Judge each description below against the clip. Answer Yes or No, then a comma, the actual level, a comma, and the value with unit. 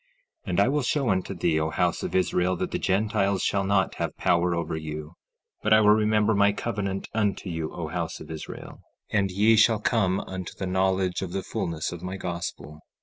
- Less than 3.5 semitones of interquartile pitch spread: Yes, average, 3.1 semitones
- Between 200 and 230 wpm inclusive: Yes, fast, 205 wpm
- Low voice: Yes, very low, 95 Hz